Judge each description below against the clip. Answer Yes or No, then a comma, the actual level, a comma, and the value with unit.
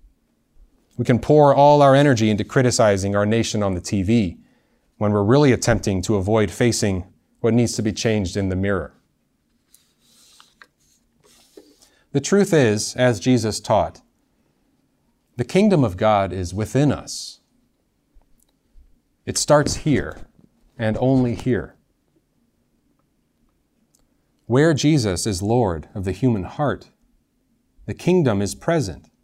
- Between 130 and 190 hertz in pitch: No, low, 110 Hz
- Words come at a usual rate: No, slow, 120 wpm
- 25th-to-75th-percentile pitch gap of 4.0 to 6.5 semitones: Yes, average, 4.4 semitones